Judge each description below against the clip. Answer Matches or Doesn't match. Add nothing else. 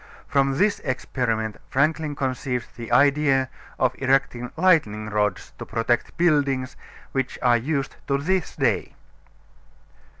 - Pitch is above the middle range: Doesn't match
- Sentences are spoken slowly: Matches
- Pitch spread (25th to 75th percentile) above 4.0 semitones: Doesn't match